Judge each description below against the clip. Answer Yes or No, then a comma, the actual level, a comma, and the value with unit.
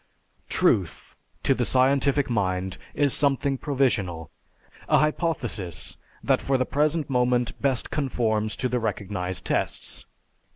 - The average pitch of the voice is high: No, low, 125 Hz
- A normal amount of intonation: No, wide, 5.7 semitones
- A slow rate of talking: Yes, slow, 120 wpm